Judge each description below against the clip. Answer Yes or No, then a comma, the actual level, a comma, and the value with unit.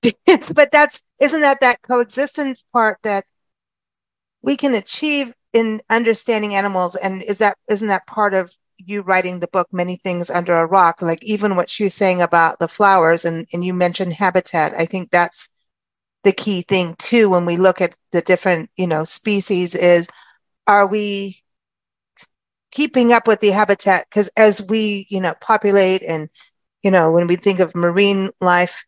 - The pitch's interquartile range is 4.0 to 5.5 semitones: No, average, 3.5 semitones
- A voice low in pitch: No, high, 195 Hz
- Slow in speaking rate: No, average, 170 wpm